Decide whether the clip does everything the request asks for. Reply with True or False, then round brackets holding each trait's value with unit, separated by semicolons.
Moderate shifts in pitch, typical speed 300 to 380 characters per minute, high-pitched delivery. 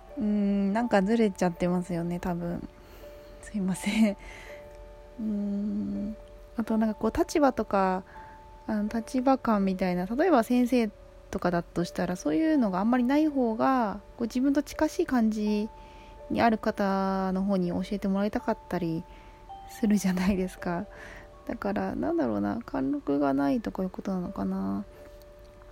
True (4.5 semitones; 310 characters per minute; 200 Hz)